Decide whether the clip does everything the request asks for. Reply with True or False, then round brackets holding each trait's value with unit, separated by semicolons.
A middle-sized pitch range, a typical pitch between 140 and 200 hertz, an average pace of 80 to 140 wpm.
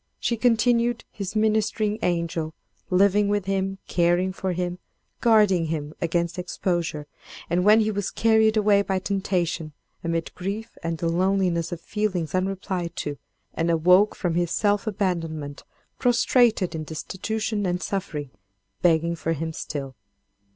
True (3.8 semitones; 185 Hz; 135 wpm)